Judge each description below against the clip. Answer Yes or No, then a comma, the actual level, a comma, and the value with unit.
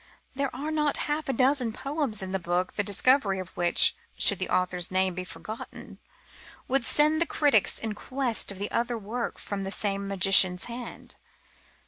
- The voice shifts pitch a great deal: Yes, wide, 6.2 semitones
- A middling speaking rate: Yes, average, 170 wpm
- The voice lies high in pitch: Yes, high, 215 Hz